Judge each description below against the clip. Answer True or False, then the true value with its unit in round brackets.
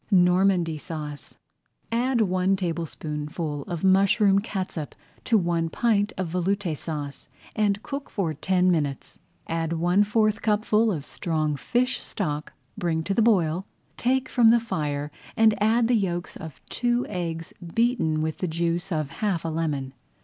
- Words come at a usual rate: True (150 wpm)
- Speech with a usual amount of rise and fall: True (4.8 semitones)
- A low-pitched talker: False (180 Hz)